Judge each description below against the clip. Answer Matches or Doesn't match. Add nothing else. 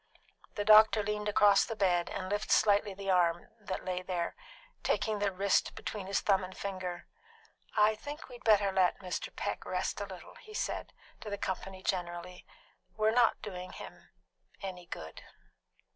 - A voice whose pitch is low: Doesn't match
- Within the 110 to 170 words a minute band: Matches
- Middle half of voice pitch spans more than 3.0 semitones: Doesn't match